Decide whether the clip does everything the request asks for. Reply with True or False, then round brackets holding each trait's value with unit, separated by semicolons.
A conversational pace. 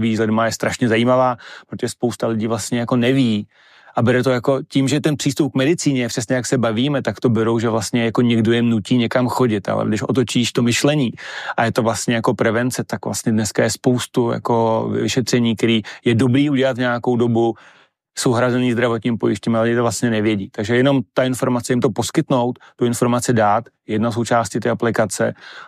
False (195 wpm)